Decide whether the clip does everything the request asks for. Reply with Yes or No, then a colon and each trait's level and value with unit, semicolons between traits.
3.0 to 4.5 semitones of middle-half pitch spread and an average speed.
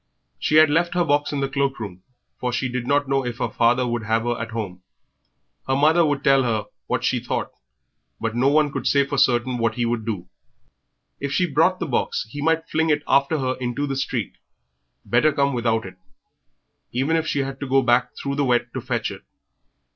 No: average, 3.3 semitones; fast, 215 wpm